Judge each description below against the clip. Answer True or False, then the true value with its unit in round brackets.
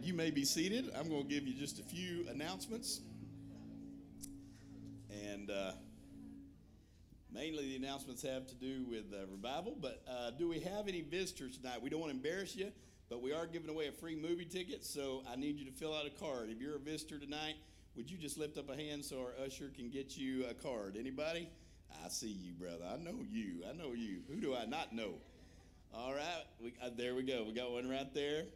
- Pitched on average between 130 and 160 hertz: True (135 Hz)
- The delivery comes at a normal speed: False (220 wpm)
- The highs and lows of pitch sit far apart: True (7.0 semitones)